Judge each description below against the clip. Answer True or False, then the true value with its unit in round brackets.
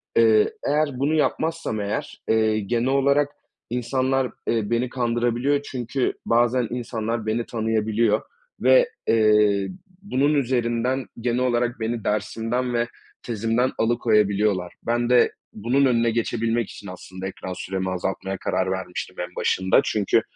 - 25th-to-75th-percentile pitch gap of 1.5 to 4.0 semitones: True (2.8 semitones)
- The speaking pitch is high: False (115 Hz)